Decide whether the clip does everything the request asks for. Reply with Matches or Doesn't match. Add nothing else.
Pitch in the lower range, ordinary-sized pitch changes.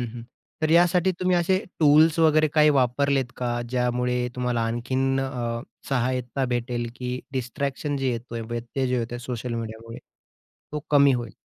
Matches